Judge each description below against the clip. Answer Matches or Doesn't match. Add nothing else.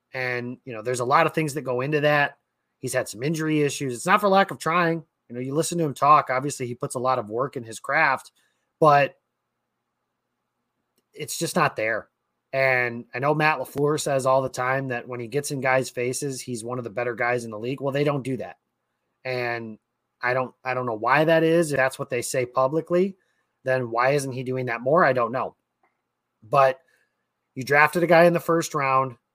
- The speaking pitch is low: Matches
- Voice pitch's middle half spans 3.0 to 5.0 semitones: Matches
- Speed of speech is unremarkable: Doesn't match